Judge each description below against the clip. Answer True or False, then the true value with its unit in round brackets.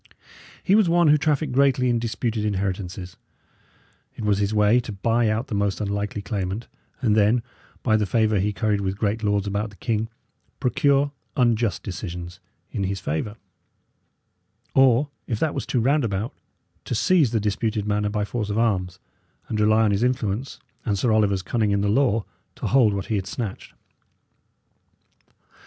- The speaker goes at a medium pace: True (170 wpm)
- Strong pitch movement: False (3.0 semitones)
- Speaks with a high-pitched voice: False (110 Hz)